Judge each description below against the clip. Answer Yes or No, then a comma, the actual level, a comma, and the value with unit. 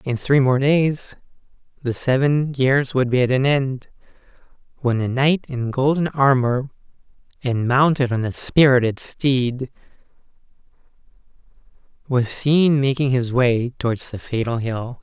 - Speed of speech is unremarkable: No, slow, 130 wpm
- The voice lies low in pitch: Yes, low, 130 Hz